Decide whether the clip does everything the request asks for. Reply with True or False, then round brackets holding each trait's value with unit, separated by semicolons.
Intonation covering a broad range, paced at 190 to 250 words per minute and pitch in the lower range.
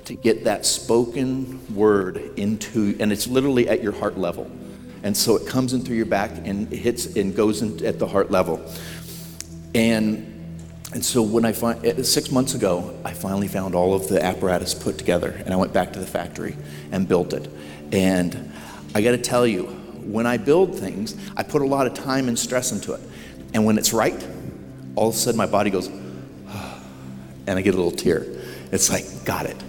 True (6.4 semitones; 200 wpm; 105 Hz)